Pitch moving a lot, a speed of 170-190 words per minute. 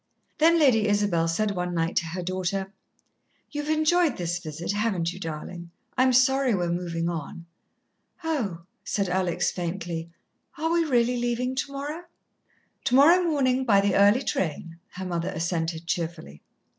No: wide, 7.2 semitones; average, 145 wpm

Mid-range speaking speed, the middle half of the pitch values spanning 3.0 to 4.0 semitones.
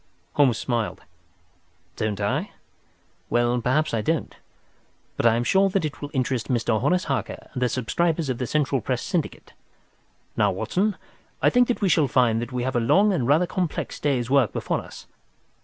No: average, 180 wpm; average, 5.3 semitones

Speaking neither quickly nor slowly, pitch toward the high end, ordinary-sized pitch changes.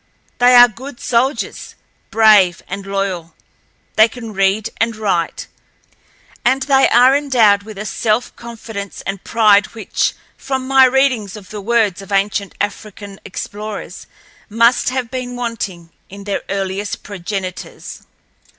No: slow, 130 wpm; high, 215 Hz; average, 3.5 semitones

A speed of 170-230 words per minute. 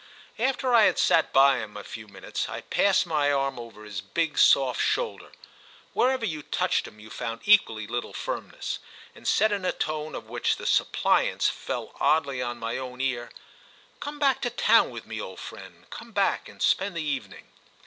Yes: average, 180 wpm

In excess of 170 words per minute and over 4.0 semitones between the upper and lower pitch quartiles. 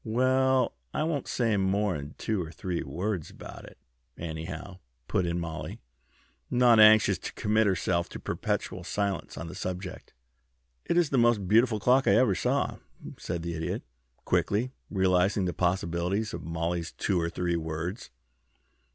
No: average, 150 wpm; average, 4.4 semitones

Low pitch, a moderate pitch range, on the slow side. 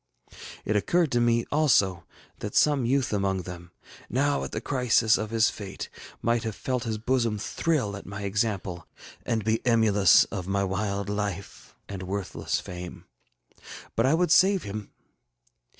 No: low, 110 Hz; average, 3.6 semitones; average, 155 wpm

